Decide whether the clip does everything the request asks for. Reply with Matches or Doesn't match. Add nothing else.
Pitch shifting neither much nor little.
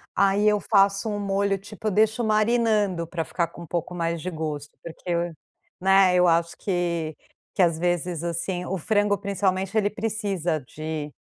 Matches